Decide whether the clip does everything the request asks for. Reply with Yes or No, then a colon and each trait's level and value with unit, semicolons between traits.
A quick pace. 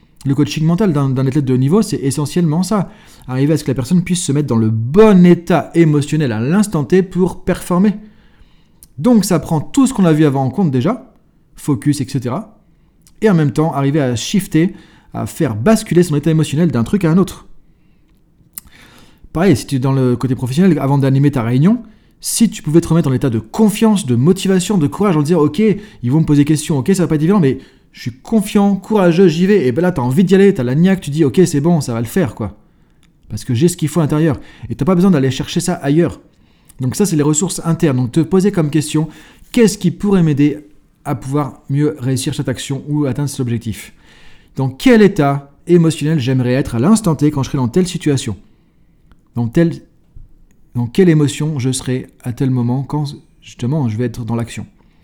Yes: fast, 225 wpm